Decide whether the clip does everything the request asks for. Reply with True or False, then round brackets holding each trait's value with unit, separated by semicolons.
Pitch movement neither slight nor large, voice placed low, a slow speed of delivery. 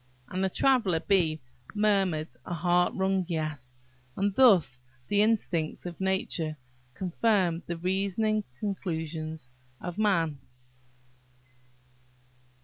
False (3.6 semitones; 180 Hz; 100 wpm)